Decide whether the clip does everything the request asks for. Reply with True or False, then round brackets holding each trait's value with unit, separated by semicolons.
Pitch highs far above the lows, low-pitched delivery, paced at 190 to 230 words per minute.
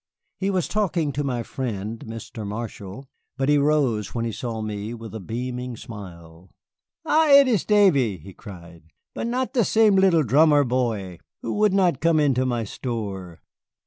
False (7.2 semitones; 125 Hz; 170 wpm)